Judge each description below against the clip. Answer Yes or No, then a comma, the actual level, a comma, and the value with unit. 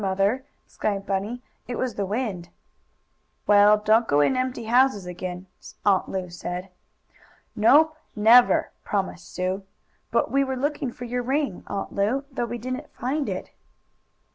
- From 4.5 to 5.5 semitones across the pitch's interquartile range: Yes, average, 4.8 semitones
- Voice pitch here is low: No, high, 220 Hz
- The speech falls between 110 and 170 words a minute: Yes, average, 145 wpm